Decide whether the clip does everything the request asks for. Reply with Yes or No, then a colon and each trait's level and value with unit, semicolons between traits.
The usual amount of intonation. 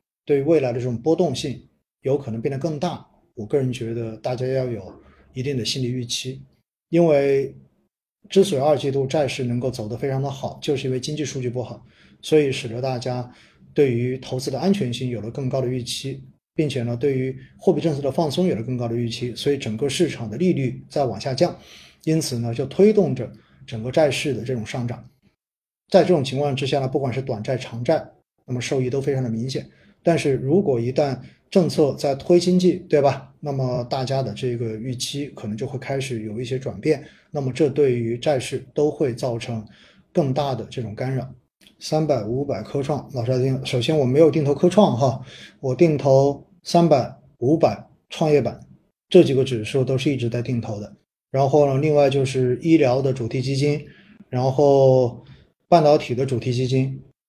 Yes: average, 3.0 semitones